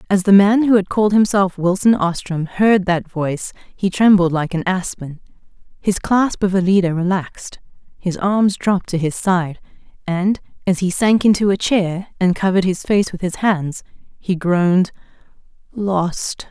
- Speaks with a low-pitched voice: No, high, 190 Hz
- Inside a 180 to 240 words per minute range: No, average, 165 wpm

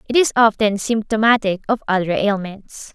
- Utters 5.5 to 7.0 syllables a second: No, 4.9 syllables/s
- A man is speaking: No, female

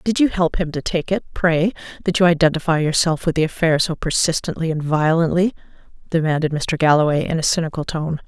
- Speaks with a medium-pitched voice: Yes, medium, 165 Hz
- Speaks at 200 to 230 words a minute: No, average, 190 wpm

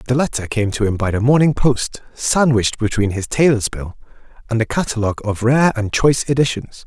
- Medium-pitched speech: No, low, 120 Hz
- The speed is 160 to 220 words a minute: Yes, average, 190 wpm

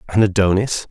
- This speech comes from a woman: No, male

